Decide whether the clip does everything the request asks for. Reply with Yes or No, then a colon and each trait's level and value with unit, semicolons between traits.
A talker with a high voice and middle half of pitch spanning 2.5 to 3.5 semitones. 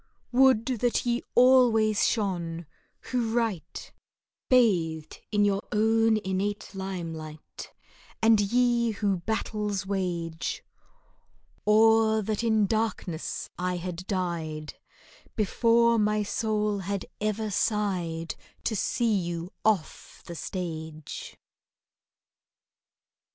No: high, 205 Hz; average, 4.1 semitones